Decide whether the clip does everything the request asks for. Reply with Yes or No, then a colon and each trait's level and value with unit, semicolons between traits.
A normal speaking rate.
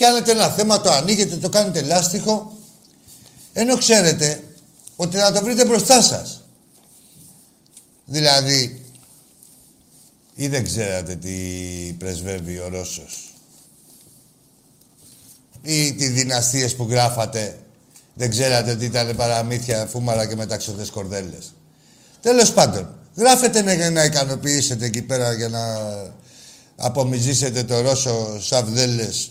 No: slow, 105 wpm